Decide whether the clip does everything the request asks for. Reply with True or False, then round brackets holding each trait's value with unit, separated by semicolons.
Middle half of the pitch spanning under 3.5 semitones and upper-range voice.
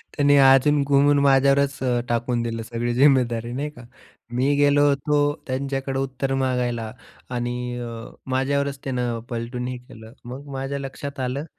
False (2.4 semitones; 135 Hz)